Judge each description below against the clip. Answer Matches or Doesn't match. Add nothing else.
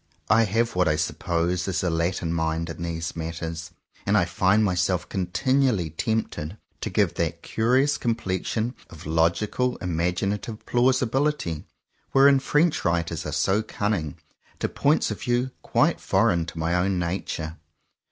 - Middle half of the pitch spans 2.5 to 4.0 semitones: Doesn't match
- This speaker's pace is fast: Doesn't match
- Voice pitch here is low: Matches